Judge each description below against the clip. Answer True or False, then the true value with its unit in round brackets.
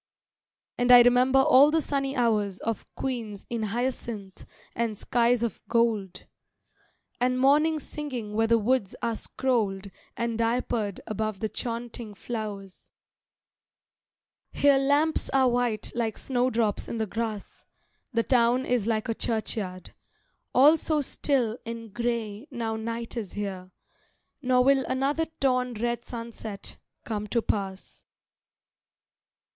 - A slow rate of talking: True (125 wpm)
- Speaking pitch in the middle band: False (235 Hz)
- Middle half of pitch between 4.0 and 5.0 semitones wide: False (2.8 semitones)